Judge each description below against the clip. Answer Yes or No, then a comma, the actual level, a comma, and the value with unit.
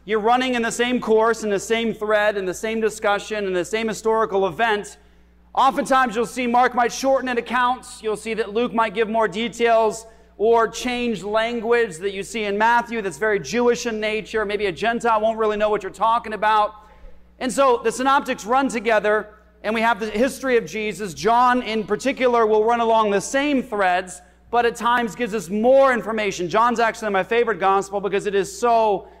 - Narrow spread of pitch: Yes, narrow, 2.0 semitones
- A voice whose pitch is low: No, high, 225 Hz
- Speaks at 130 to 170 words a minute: No, average, 195 wpm